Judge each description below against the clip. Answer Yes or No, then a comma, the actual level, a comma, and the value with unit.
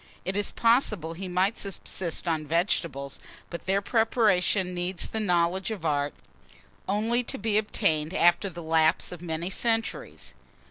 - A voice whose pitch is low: No, medium, 180 Hz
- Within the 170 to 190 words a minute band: No, average, 145 wpm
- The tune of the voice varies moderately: Yes, average, 3.9 semitones